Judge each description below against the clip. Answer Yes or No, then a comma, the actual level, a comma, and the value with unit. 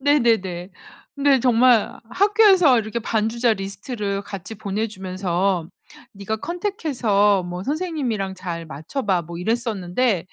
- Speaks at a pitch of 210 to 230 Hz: Yes, high, 215 Hz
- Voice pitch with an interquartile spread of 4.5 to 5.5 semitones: Yes, average, 5.1 semitones